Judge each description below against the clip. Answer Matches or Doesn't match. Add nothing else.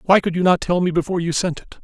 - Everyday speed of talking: Doesn't match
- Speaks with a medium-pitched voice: Matches